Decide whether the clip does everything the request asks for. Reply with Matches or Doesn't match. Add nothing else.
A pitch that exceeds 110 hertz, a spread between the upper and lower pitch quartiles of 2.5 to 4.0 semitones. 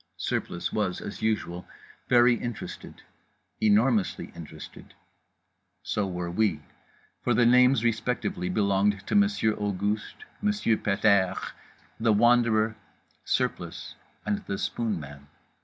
Doesn't match